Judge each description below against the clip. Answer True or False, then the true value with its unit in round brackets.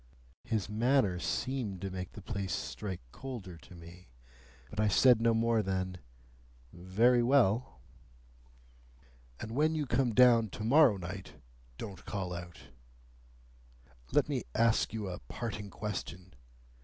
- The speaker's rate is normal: False (130 wpm)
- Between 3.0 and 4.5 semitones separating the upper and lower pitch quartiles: True (4.2 semitones)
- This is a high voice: False (105 Hz)